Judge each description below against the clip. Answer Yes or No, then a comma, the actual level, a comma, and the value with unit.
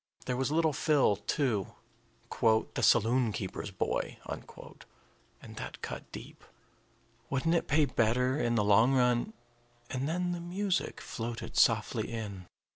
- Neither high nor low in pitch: No, low, 125 Hz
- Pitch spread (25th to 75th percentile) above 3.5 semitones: Yes, average, 5.3 semitones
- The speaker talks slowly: Yes, slow, 130 wpm